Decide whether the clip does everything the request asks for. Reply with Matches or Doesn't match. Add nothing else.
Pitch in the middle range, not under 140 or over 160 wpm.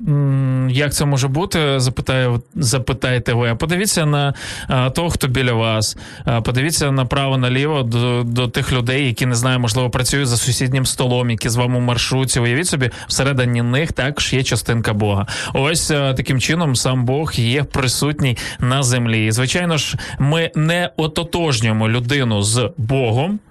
Doesn't match